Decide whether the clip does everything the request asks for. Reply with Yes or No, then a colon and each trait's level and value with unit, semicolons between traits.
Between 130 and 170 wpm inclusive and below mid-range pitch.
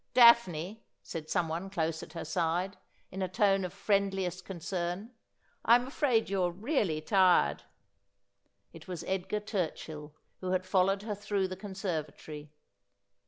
No: average, 140 wpm; medium, 185 Hz